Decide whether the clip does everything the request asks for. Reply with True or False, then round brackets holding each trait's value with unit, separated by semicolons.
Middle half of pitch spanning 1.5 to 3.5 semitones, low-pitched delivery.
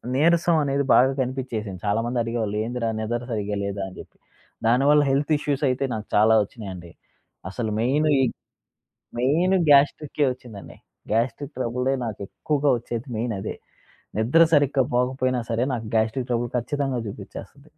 False (4.0 semitones; 125 Hz)